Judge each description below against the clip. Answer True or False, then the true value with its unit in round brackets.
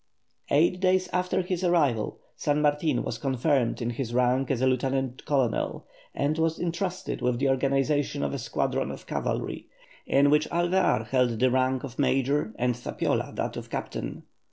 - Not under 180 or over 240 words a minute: False (165 wpm)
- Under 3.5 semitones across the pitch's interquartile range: False (4.1 semitones)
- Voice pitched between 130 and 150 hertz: True (140 Hz)